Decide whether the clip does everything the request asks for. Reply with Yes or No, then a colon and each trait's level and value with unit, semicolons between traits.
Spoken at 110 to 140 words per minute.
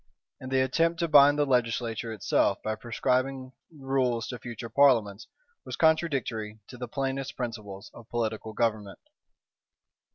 Yes: slow, 135 wpm